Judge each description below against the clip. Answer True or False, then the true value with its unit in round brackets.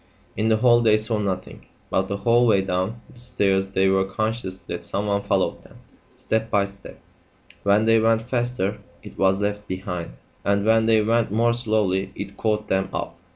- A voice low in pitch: True (105 Hz)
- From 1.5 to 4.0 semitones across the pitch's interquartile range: True (2.7 semitones)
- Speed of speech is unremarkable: True (185 wpm)